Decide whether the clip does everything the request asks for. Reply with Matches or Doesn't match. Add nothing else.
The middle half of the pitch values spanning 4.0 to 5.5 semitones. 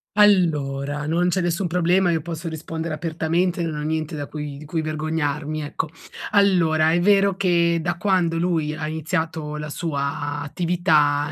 Doesn't match